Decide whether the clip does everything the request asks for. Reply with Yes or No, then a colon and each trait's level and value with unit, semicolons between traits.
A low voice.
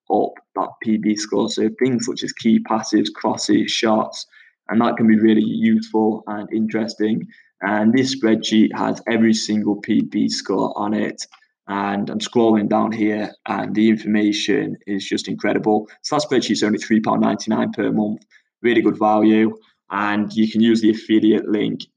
Yes: low, 110 Hz